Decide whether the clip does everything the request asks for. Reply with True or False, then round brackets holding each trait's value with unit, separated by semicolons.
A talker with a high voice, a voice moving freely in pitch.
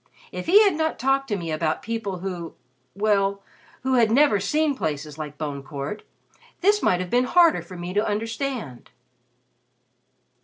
True (205 Hz; 7.9 semitones)